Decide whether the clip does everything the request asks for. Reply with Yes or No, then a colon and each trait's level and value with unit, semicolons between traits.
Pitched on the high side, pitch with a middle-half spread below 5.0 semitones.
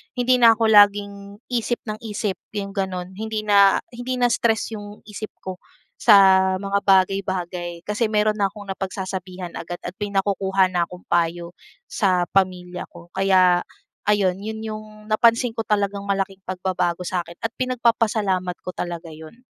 Yes: high, 195 Hz; average, 2.8 semitones